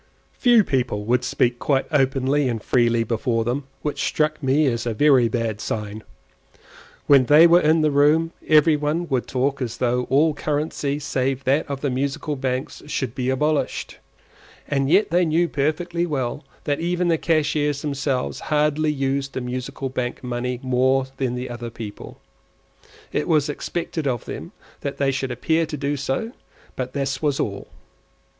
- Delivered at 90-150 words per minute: No, average, 165 wpm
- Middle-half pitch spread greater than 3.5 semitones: No, average, 3.1 semitones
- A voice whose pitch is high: No, medium, 140 Hz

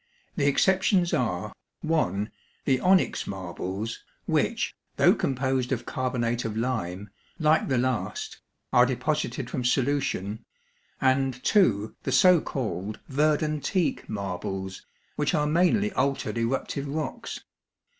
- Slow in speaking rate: Yes, slow, 115 wpm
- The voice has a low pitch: Yes, low, 130 Hz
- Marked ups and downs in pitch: Yes, wide, 6.0 semitones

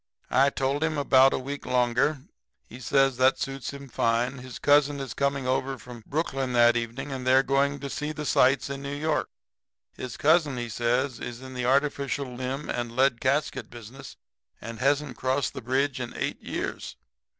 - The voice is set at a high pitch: No, low, 135 Hz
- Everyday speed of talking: Yes, average, 185 wpm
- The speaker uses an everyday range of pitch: No, narrow, 2.1 semitones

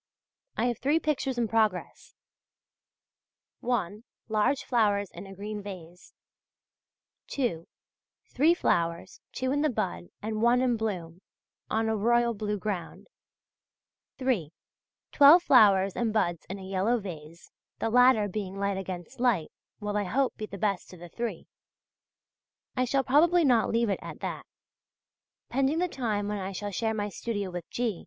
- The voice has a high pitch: Yes, high, 215 Hz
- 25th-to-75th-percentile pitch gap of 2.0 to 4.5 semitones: Yes, average, 4.1 semitones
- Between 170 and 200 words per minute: No, average, 155 wpm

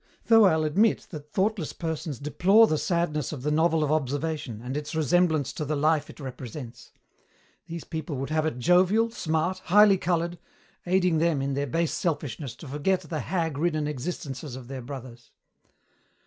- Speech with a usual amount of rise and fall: Yes, average, 3.5 semitones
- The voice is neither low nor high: Yes, medium, 155 Hz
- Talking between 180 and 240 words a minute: No, average, 170 wpm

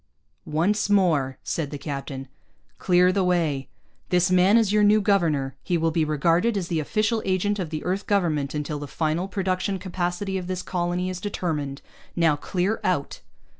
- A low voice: No, medium, 180 Hz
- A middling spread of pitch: Yes, average, 3.9 semitones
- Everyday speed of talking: Yes, average, 170 wpm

